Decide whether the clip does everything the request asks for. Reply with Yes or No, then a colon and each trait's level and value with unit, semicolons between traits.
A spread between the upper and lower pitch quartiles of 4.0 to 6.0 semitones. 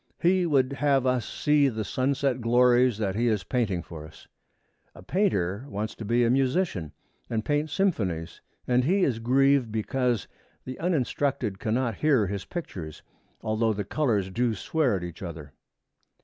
Yes: average, 5.2 semitones